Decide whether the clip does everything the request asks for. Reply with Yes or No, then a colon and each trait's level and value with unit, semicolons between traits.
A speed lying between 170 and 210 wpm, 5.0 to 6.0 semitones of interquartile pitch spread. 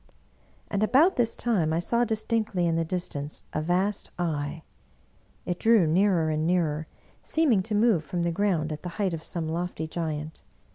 No: average, 175 wpm; average, 4.6 semitones